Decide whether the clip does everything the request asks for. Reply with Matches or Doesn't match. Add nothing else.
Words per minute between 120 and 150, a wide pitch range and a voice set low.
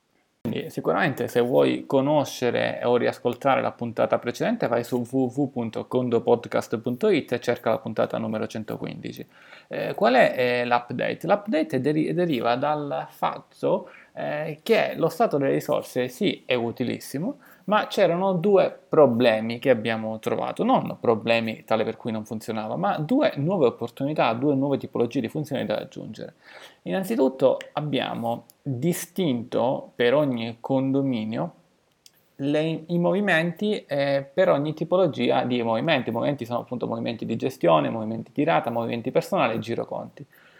Matches